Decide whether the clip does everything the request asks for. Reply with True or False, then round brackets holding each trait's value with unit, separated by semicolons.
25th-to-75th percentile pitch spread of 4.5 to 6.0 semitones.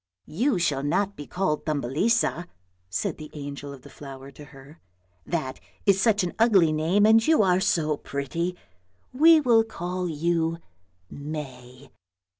True (5.6 semitones)